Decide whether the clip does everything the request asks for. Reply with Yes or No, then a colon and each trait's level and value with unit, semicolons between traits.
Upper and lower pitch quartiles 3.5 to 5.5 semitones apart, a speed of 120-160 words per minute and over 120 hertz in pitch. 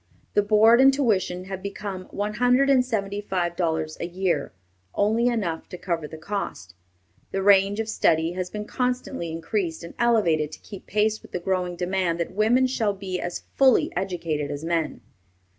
No: average, 4.0 semitones; average, 175 wpm; high, 190 Hz